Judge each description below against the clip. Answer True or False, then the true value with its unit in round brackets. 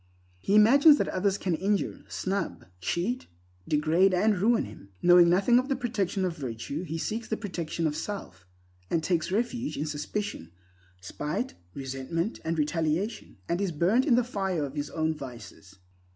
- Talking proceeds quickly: False (165 wpm)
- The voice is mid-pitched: True (180 Hz)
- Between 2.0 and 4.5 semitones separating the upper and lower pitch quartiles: False (5.5 semitones)